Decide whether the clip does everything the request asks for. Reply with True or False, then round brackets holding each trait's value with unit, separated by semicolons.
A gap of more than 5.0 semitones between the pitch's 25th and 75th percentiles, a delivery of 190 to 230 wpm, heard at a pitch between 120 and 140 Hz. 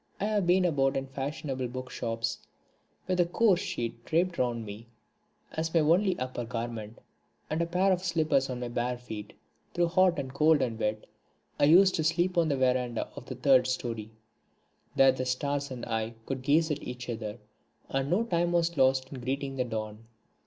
True (5.6 semitones; 195 wpm; 135 Hz)